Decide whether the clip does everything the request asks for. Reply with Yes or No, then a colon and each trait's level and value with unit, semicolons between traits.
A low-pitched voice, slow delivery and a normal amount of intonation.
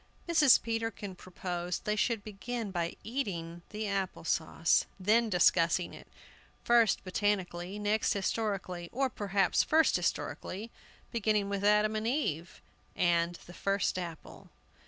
No: high, 200 Hz; slow, 125 wpm; average, 3.7 semitones